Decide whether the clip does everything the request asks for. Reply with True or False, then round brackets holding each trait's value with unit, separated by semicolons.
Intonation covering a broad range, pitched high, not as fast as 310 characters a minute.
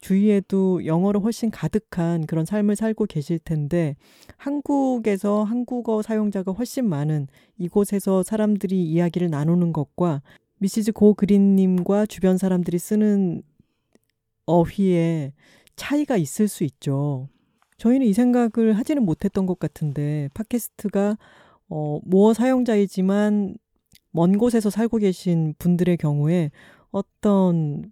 False (4.2 semitones; 195 Hz; 275 characters per minute)